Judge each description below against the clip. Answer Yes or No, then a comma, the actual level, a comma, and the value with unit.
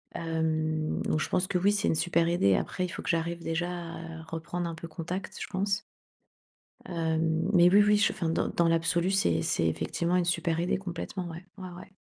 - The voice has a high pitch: No, medium, 170 Hz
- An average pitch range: No, narrow, 1.9 semitones